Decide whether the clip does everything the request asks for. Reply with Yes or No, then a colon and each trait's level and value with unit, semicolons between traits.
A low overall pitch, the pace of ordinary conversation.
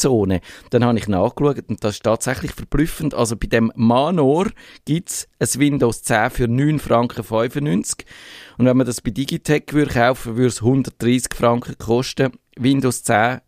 Yes: low, 125 Hz; average, 170 wpm